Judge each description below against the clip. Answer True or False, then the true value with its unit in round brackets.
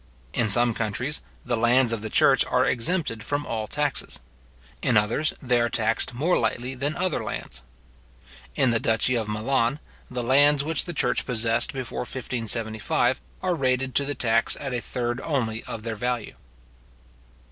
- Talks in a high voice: False (120 Hz)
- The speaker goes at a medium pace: True (165 wpm)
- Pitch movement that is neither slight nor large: True (3.2 semitones)